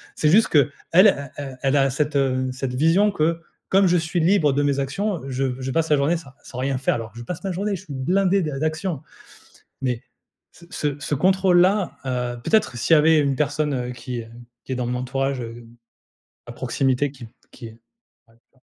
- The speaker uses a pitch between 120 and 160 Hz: Yes, medium, 140 Hz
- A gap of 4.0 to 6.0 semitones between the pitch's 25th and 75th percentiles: Yes, average, 4.7 semitones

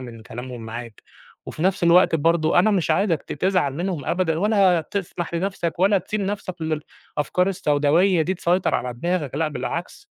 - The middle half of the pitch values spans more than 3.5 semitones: Yes, average, 4.1 semitones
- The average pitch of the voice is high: No, medium, 170 Hz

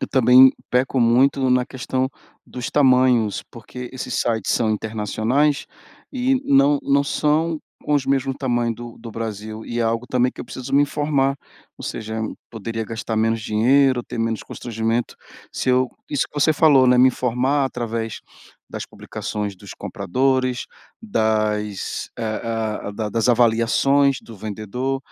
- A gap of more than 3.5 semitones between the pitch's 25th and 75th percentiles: No, average, 3.2 semitones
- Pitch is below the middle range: Yes, low, 125 Hz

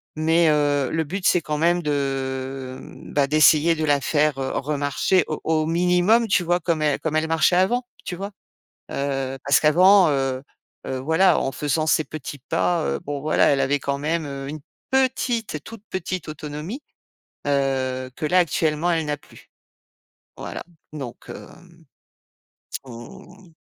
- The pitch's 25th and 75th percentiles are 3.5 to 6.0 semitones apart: Yes, average, 3.9 semitones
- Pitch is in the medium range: Yes, medium, 155 Hz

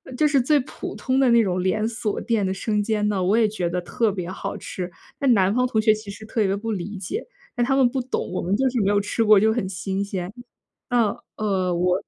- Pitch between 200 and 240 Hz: Yes, high, 210 Hz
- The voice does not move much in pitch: No, average, 3.7 semitones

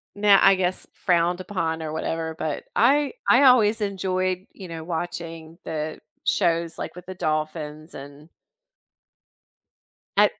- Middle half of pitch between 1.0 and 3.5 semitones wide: Yes, average, 2.9 semitones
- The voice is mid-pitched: Yes, medium, 170 Hz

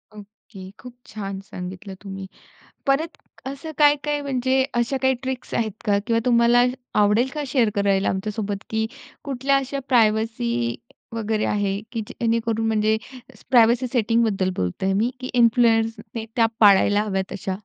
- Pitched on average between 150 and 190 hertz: No, high, 225 Hz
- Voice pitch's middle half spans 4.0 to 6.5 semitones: No, average, 3.6 semitones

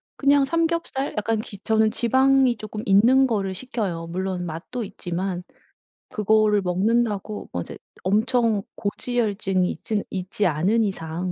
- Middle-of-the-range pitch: No, high, 210 Hz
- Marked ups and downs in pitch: No, average, 4.2 semitones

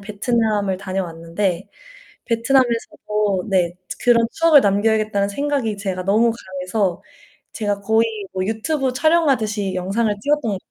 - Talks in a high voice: Yes, high, 210 Hz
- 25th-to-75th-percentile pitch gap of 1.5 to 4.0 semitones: Yes, average, 3.3 semitones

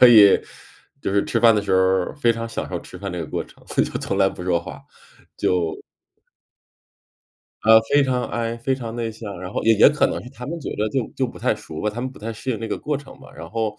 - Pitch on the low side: Yes, low, 115 Hz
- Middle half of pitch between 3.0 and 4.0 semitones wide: Yes, average, 3.5 semitones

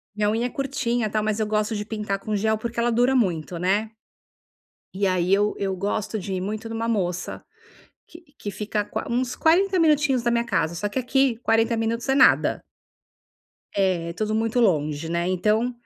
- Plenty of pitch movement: No, average, 3.2 semitones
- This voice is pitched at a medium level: No, high, 215 Hz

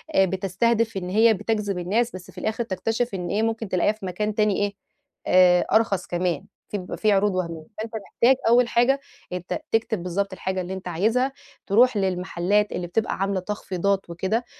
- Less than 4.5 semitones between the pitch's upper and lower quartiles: Yes, average, 3.5 semitones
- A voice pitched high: Yes, high, 200 Hz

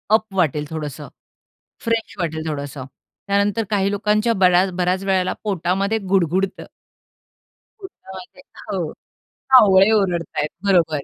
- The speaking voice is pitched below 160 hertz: No, high, 190 Hz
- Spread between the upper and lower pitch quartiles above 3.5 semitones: No, average, 3.2 semitones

